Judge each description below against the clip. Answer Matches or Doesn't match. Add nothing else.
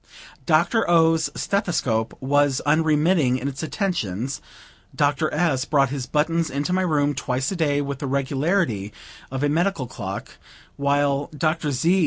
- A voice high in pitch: Doesn't match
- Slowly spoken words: Doesn't match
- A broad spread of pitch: Doesn't match